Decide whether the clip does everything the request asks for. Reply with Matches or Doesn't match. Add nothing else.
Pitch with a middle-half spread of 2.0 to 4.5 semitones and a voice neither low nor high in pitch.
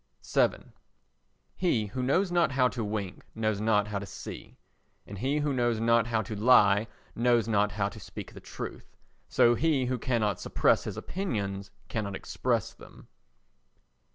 Doesn't match